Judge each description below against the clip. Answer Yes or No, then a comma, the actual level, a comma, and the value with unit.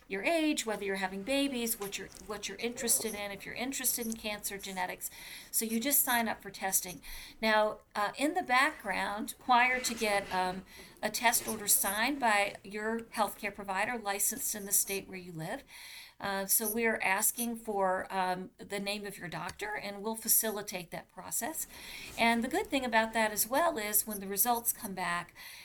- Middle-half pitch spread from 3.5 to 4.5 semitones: No, average, 3.0 semitones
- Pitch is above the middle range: Yes, high, 210 Hz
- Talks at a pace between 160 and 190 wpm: Yes, average, 185 wpm